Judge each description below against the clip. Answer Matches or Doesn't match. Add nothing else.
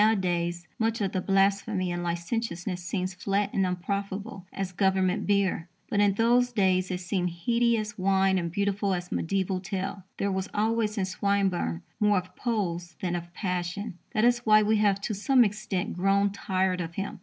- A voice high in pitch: Matches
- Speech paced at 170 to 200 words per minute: Matches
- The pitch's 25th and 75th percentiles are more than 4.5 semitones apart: Doesn't match